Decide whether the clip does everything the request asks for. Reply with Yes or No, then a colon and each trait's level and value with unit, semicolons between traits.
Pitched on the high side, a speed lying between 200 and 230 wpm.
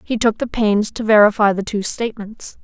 Yes: high, 215 Hz; fast, 205 wpm